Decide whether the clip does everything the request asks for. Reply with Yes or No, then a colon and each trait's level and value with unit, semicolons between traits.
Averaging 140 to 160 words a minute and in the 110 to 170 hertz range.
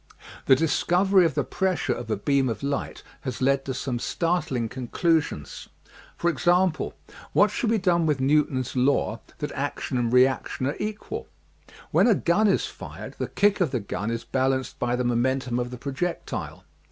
No: average, 175 wpm; low, 135 Hz